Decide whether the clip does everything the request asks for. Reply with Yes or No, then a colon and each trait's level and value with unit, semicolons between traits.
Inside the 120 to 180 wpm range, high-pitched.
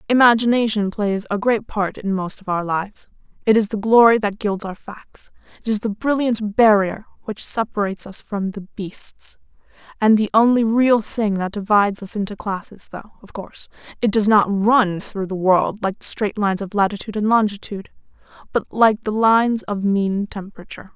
Yes: average, 175 wpm; high, 210 Hz